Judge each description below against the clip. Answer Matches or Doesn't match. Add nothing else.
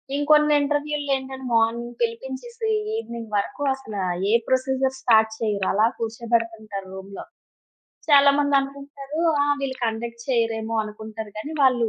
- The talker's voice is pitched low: Doesn't match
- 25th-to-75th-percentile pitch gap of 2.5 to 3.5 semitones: Doesn't match